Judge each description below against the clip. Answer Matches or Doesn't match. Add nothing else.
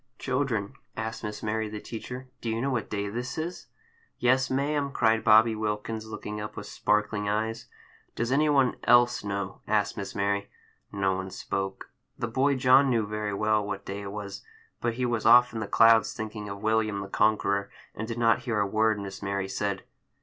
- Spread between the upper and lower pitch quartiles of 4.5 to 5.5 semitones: Doesn't match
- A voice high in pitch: Doesn't match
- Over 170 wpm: Matches